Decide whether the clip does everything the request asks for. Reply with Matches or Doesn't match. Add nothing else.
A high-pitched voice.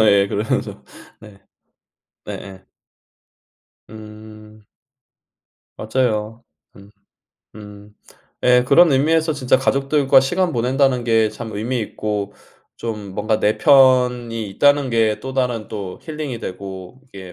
Doesn't match